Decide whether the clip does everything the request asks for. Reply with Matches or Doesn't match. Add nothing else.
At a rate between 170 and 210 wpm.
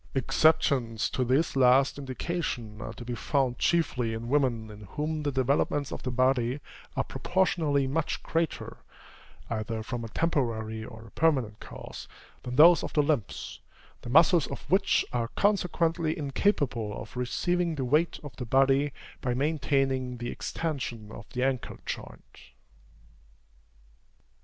Doesn't match